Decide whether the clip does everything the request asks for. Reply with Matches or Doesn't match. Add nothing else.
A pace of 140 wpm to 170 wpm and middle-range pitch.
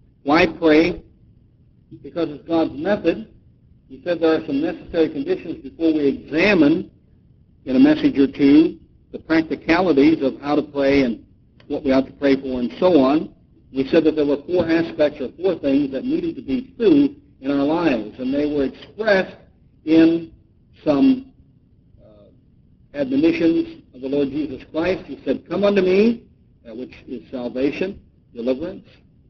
Matches